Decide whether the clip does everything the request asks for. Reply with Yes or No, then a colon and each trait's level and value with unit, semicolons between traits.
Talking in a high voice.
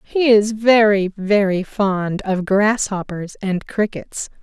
Yes: high, 200 Hz